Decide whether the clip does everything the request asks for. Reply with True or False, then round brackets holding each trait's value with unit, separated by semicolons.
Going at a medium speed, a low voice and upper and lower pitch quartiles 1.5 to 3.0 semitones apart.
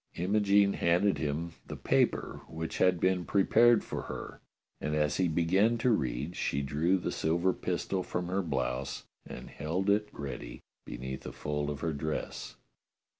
False (160 wpm; 85 Hz; 4.7 semitones)